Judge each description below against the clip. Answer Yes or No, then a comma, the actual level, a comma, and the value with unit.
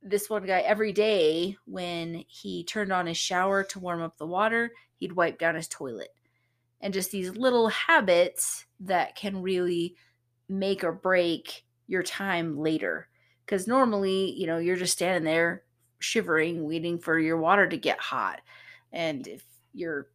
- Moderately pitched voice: Yes, medium, 180 Hz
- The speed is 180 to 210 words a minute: No, average, 160 wpm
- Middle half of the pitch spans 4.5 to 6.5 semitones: No, average, 3.5 semitones